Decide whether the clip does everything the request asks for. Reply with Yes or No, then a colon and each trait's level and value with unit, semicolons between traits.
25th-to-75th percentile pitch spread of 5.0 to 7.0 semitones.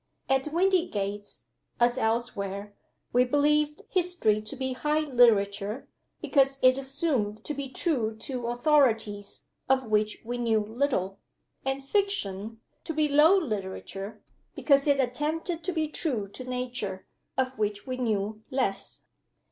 Yes: wide, 5.4 semitones